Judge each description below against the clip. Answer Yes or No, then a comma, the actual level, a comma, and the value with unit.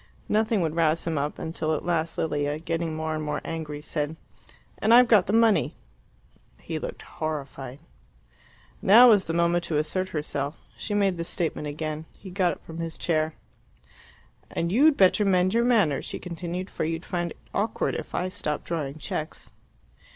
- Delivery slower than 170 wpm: No, average, 175 wpm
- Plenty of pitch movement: No, average, 3.4 semitones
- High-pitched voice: No, medium, 165 Hz